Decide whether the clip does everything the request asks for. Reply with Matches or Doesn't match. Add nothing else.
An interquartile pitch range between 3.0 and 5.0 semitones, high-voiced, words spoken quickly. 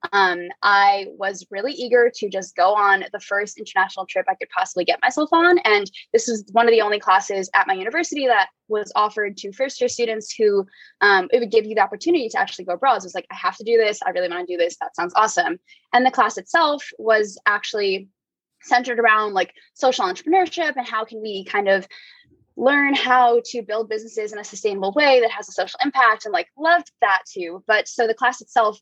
Matches